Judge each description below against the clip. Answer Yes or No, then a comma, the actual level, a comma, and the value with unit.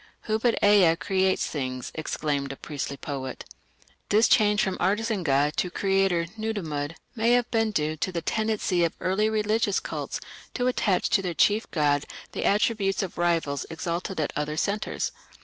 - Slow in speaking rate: No, average, 165 wpm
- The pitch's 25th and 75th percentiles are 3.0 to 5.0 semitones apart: No, wide, 5.6 semitones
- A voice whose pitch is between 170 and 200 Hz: Yes, medium, 185 Hz